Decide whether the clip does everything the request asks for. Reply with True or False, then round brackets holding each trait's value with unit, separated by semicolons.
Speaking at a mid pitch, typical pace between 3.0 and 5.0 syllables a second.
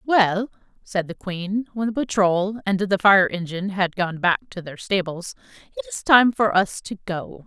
False (200 Hz; 4.5 syllables/s)